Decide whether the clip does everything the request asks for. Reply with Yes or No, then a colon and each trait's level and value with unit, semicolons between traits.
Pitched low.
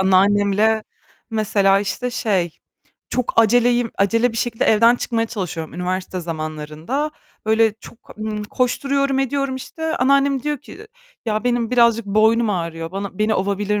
No: high, 220 Hz